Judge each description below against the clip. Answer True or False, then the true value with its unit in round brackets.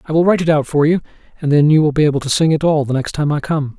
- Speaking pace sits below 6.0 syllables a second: False (7.3 syllables/s)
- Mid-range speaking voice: True (150 Hz)